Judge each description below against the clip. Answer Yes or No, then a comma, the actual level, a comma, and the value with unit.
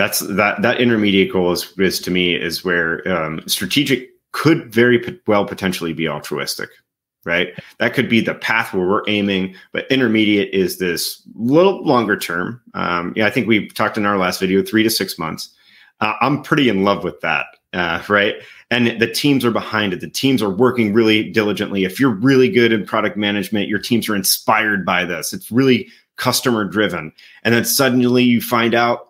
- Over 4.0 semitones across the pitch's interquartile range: No, average, 3.5 semitones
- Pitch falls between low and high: No, low, 110 Hz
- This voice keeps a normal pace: Yes, average, 195 wpm